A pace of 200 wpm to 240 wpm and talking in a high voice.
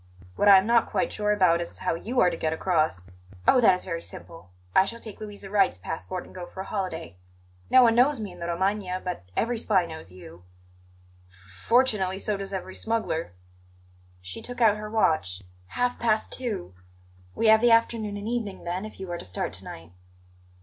Yes: fast, 205 wpm; high, 195 Hz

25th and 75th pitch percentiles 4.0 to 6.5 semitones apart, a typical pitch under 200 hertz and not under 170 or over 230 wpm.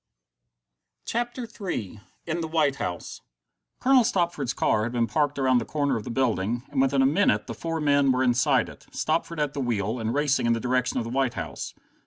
Yes: average, 4.6 semitones; low, 135 Hz; fast, 205 wpm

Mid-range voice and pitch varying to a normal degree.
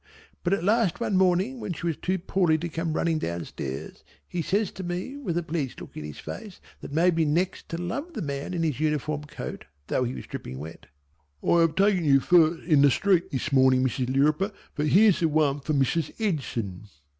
Yes: medium, 165 Hz; average, 4.6 semitones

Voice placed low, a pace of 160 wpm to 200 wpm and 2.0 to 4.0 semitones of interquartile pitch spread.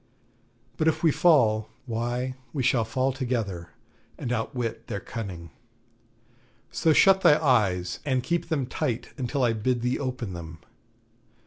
No: low, 125 Hz; average, 140 wpm; average, 3.3 semitones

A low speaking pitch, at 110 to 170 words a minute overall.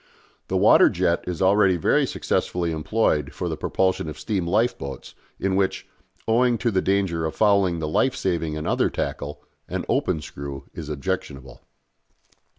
Yes: very low, 85 Hz; average, 155 wpm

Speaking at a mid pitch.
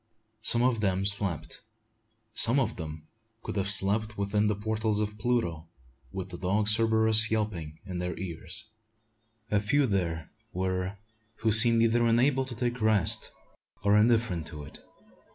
No: low, 105 Hz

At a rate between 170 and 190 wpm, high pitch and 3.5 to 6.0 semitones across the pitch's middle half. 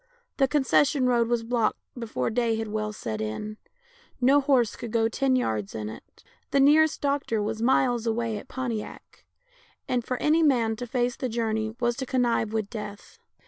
No: average, 180 wpm; high, 235 Hz; average, 2.9 semitones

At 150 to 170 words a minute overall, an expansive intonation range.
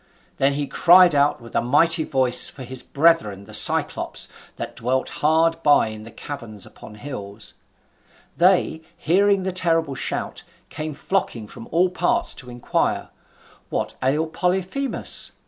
No: average, 140 wpm; wide, 5.7 semitones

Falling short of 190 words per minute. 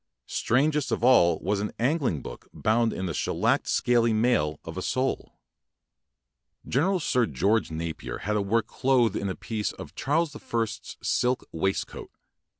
Yes: average, 165 wpm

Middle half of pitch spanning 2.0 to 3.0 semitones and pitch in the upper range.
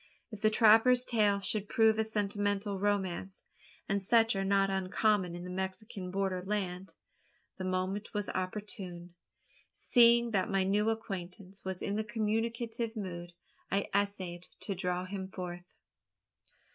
Yes: narrow, 2.6 semitones; high, 200 Hz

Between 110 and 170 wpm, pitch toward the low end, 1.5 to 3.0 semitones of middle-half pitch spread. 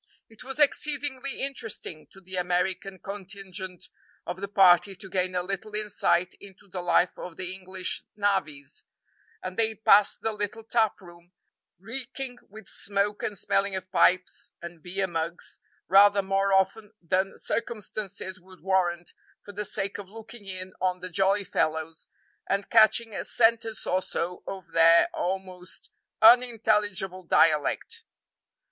No: average, 140 wpm; high, 195 Hz; narrow, 2.5 semitones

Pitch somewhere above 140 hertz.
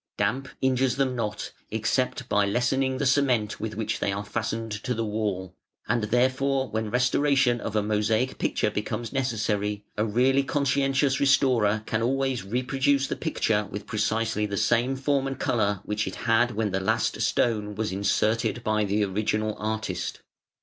No: low, 115 Hz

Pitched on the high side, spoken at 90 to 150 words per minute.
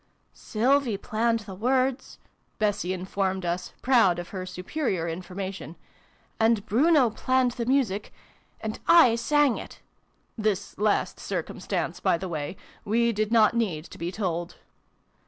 Yes: high, 215 Hz; average, 140 wpm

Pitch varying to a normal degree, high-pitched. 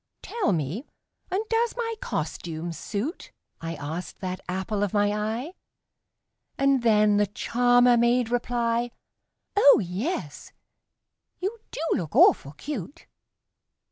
No: wide, 6.8 semitones; high, 225 Hz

